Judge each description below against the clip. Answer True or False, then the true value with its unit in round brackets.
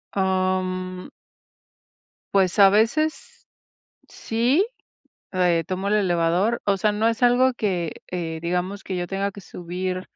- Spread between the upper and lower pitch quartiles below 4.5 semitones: True (2.7 semitones)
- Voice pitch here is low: False (190 Hz)